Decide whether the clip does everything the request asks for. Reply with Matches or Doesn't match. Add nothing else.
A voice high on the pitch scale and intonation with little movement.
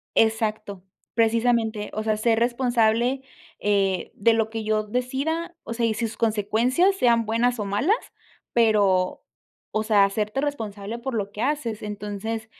Matches